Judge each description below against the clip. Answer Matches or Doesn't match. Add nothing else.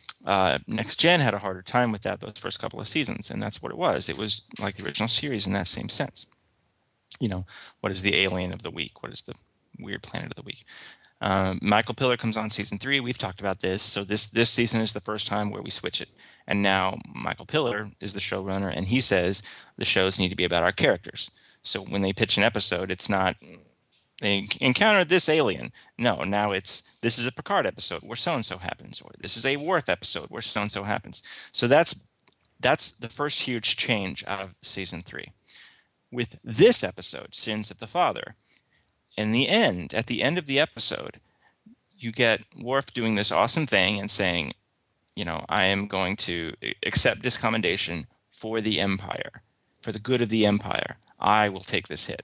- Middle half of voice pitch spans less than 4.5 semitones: Matches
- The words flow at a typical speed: Doesn't match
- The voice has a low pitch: Matches